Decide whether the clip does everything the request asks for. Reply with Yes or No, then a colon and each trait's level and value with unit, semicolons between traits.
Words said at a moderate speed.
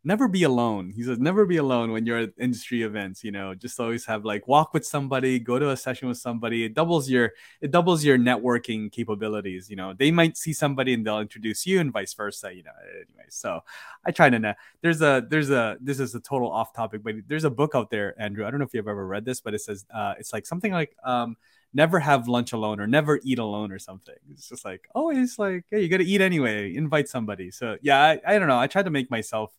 No: fast, 250 wpm